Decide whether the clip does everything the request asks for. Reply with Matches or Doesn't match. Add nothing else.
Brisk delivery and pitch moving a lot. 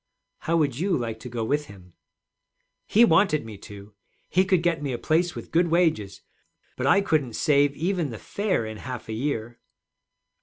Doesn't match